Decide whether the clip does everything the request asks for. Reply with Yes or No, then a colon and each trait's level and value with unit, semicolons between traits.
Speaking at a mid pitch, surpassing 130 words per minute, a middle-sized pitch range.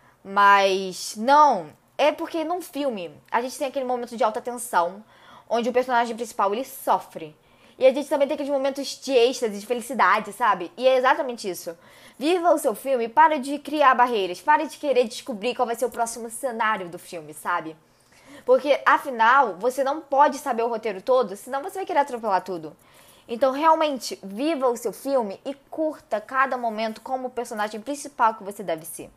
No: very high, 250 Hz; fast, 185 wpm; average, 4.4 semitones